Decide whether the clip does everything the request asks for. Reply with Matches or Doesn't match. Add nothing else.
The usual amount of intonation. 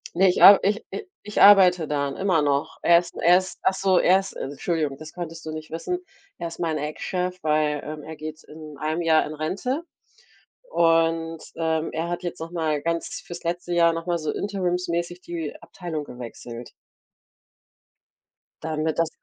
Doesn't match